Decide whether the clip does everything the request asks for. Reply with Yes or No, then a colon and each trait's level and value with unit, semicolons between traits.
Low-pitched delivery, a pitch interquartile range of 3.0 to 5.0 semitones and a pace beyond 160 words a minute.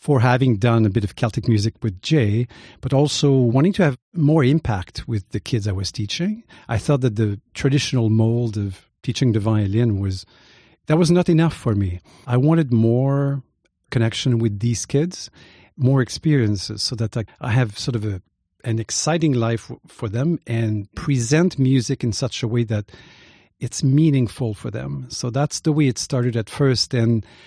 Yes: low, 120 Hz; average, 3.9 semitones; average, 180 wpm